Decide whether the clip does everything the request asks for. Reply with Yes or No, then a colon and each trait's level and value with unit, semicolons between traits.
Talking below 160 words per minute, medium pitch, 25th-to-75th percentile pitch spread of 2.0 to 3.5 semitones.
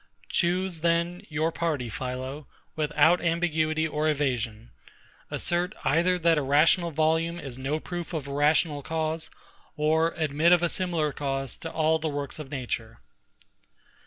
Yes: average, 145 wpm; medium, 155 Hz; average, 2.7 semitones